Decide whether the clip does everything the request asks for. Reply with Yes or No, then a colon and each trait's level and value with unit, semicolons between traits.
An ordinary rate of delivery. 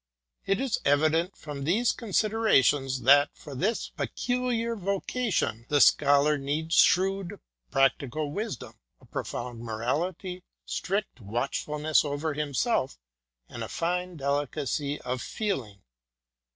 No: slow, 110 wpm